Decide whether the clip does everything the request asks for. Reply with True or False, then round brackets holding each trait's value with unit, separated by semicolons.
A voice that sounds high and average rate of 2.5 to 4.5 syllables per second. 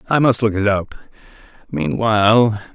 False (110 Hz; 4.4 syllables/s)